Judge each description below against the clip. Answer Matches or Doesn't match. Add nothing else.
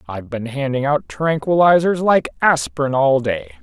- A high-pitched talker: Doesn't match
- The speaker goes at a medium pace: Matches